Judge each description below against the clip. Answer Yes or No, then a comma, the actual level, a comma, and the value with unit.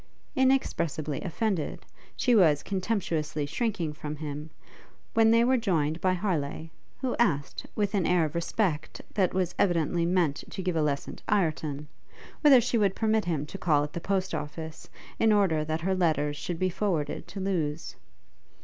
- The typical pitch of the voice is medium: Yes, medium, 175 Hz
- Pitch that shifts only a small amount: No, average, 4.7 semitones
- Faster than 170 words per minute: No, average, 165 wpm